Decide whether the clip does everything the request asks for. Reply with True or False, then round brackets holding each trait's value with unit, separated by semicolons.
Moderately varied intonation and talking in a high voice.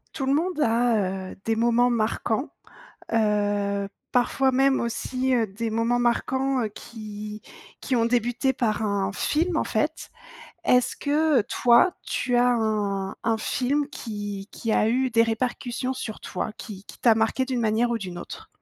True (3.2 semitones; 235 Hz)